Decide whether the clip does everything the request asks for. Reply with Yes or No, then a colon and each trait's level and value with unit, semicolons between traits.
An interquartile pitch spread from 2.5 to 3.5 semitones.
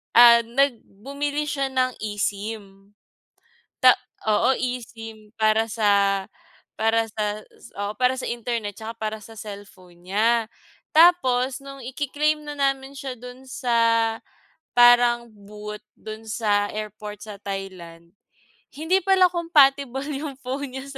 No: average, 4.3 semitones